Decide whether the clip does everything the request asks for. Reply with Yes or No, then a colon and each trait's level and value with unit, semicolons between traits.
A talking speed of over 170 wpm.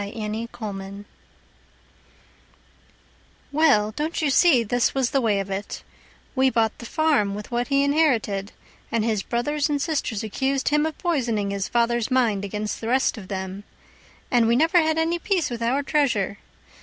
No: average, 165 wpm